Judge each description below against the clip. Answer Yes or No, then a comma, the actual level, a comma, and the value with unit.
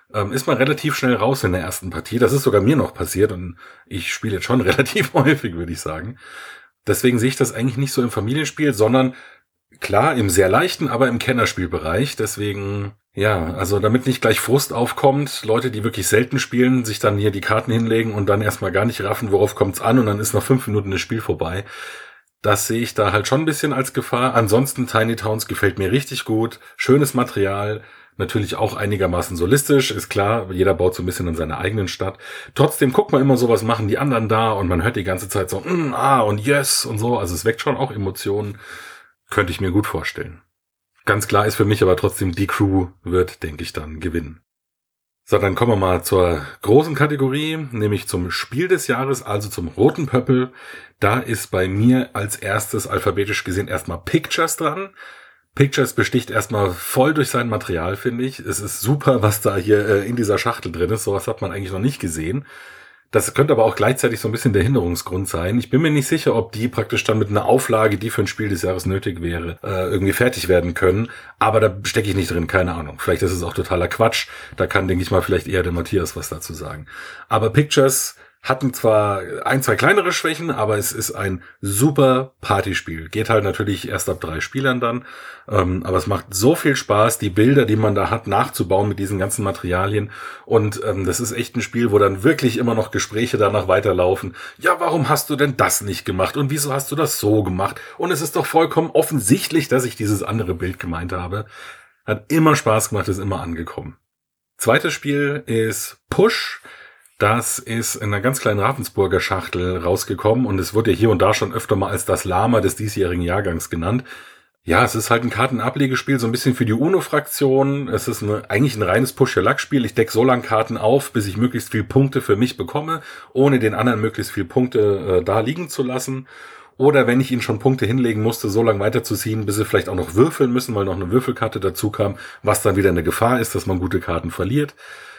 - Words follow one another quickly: Yes, fast, 210 wpm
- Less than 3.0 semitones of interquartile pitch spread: No, average, 4.8 semitones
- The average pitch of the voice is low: Yes, low, 110 Hz